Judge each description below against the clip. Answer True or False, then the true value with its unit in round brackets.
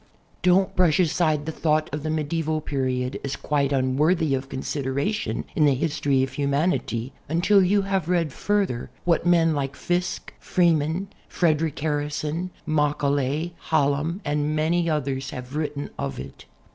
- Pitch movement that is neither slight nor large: True (3.4 semitones)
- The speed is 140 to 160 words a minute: True (145 wpm)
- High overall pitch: False (150 Hz)